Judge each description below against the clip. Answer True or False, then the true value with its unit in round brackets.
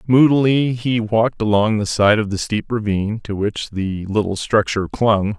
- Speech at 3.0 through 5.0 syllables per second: True (4.8 syllables/s)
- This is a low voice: True (110 Hz)